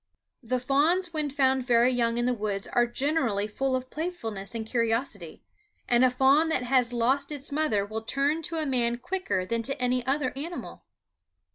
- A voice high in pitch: Yes, very high, 255 Hz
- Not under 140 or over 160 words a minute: No, average, 180 wpm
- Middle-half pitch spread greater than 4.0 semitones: No, average, 3.5 semitones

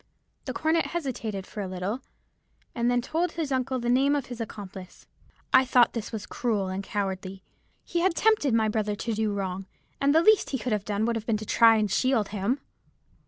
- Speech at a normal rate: No, fast, 210 wpm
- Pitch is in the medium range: No, high, 225 Hz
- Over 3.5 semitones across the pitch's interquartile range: Yes, average, 4.4 semitones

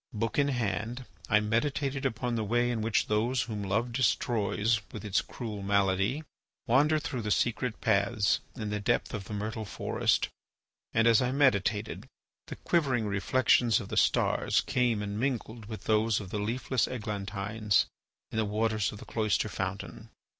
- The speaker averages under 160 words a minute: No, average, 165 wpm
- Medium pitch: No, low, 110 Hz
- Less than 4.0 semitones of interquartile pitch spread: Yes, average, 2.8 semitones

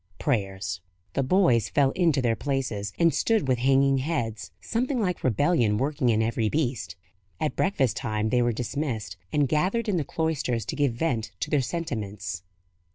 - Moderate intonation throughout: No, wide, 5.9 semitones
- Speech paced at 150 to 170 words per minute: Yes, average, 165 wpm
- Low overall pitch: Yes, low, 130 Hz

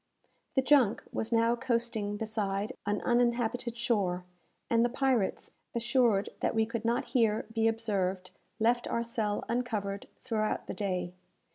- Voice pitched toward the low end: No, high, 225 Hz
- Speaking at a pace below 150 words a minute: Yes, average, 140 wpm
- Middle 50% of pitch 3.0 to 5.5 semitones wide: No, narrow, 2.5 semitones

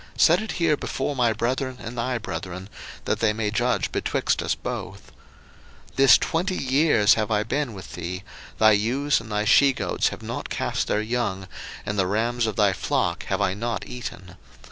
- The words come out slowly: No, average, 190 wpm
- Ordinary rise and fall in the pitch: Yes, average, 3.9 semitones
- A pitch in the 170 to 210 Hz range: No, low, 115 Hz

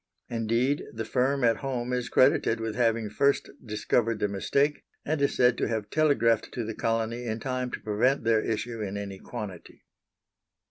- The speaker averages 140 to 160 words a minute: No, average, 175 wpm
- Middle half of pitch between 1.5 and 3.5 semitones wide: Yes, narrow, 2.6 semitones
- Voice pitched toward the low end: Yes, low, 115 Hz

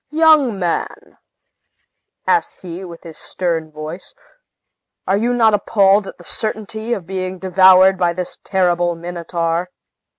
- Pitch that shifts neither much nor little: Yes, average, 3.2 semitones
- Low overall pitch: No, medium, 185 Hz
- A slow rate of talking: Yes, slow, 130 wpm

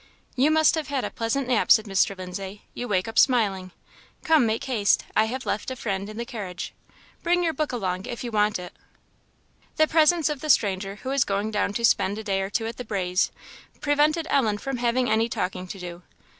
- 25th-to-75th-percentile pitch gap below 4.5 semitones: No, average, 5.1 semitones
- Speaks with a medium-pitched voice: No, high, 225 Hz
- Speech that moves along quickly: Yes, fast, 215 wpm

